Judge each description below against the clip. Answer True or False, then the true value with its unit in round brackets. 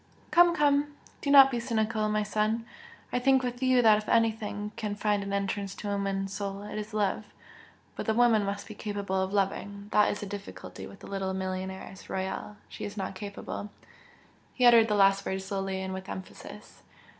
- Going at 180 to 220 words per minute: True (195 wpm)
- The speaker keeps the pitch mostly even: True (2.2 semitones)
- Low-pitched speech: False (205 Hz)